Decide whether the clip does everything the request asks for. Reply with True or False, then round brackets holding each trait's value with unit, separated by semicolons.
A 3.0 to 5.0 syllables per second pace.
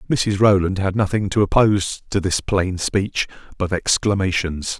True (4.5 syllables/s)